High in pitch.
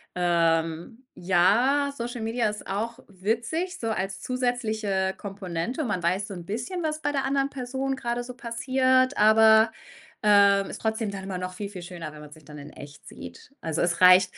Yes: high, 210 Hz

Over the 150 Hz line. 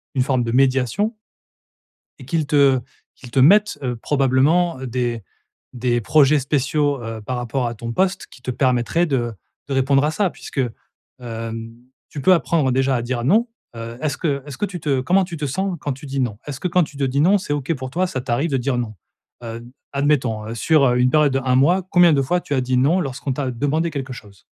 No: low, 135 Hz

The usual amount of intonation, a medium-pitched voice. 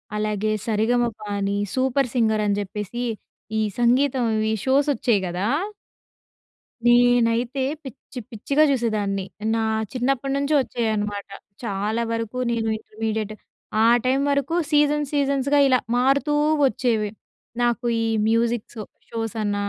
No: average, 3.6 semitones; high, 235 Hz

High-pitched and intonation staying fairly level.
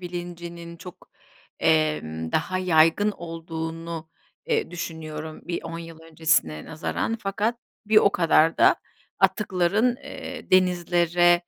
No: medium, 170 Hz; narrow, 2.2 semitones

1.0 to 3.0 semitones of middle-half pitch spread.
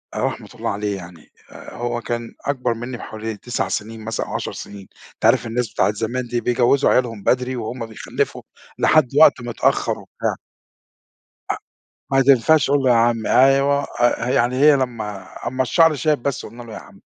Yes: narrow, 2.6 semitones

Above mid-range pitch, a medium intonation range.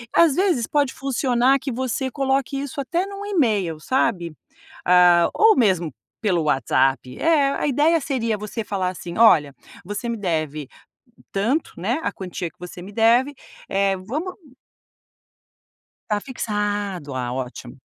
No: high, 215 Hz; wide, 7.5 semitones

